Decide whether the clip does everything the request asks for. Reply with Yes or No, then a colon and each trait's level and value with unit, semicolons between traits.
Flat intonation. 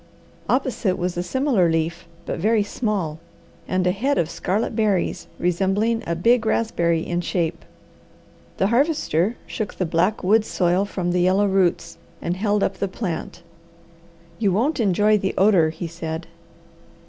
No: average, 3.8 semitones